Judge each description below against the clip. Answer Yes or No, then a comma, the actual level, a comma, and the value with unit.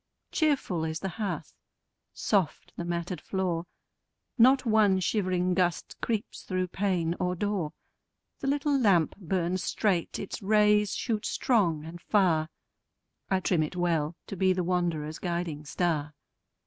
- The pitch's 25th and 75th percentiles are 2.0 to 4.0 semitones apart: Yes, average, 3.4 semitones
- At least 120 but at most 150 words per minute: Yes, slow, 135 wpm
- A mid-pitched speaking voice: Yes, medium, 180 Hz